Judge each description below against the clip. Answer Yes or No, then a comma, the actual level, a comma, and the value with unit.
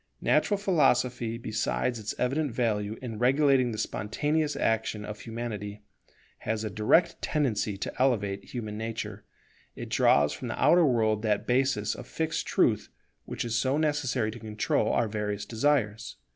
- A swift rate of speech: No, average, 150 wpm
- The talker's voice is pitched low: Yes, low, 115 Hz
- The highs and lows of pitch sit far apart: No, average, 3.9 semitones